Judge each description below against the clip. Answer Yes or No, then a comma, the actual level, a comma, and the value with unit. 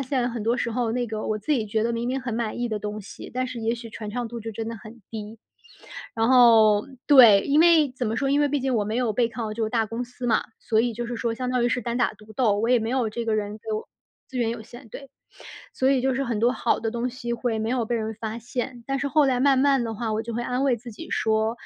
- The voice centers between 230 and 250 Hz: Yes, high, 235 Hz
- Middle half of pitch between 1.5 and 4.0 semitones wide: Yes, narrow, 2.4 semitones